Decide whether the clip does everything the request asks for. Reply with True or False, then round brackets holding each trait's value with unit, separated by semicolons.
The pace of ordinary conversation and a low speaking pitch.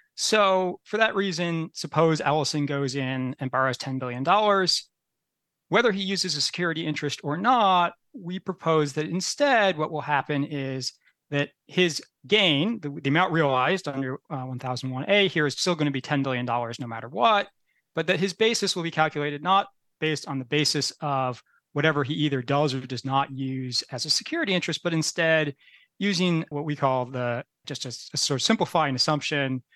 False (175 wpm; 150 Hz)